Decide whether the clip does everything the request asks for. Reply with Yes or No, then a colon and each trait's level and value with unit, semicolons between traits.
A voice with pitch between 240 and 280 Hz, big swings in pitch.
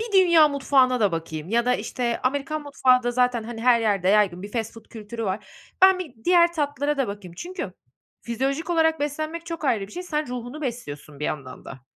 Yes: very high, 250 Hz; wide, 6.5 semitones